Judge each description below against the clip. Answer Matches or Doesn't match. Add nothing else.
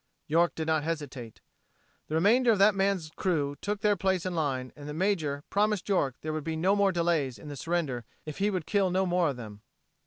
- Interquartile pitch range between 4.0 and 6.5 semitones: Matches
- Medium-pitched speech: Matches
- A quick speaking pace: Matches